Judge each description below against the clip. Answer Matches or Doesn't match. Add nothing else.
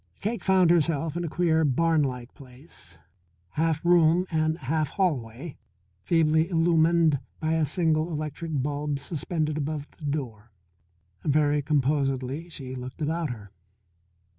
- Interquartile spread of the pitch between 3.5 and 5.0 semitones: Doesn't match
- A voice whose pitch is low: Doesn't match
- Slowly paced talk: Matches